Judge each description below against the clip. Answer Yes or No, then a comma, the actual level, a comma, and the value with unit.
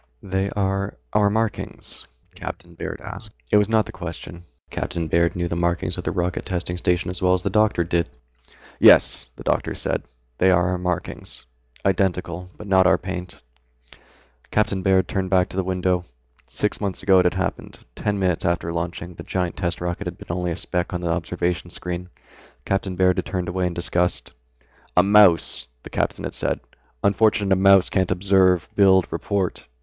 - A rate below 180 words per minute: No, average, 185 wpm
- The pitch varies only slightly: Yes, narrow, 1.7 semitones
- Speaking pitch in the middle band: No, very low, 90 Hz